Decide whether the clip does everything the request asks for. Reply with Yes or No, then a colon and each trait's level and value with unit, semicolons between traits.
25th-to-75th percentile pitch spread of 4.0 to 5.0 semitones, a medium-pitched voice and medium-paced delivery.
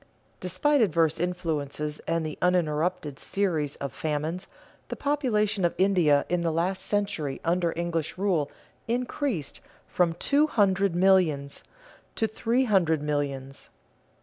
No: average, 4.5 semitones; medium, 175 Hz; slow, 120 wpm